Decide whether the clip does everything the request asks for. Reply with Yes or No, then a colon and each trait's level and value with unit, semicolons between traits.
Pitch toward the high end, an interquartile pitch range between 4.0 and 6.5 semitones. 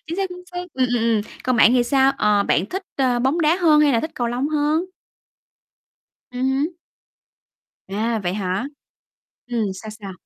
Yes: very high, 255 Hz; average, 5.3 semitones